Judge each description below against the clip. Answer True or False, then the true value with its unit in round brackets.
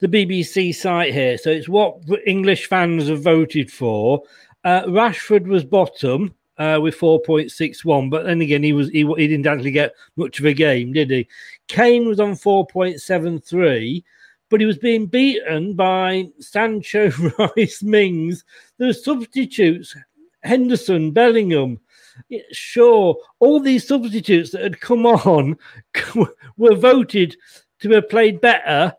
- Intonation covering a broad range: True (5.9 semitones)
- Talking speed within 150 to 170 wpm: False (135 wpm)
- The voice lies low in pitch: False (185 Hz)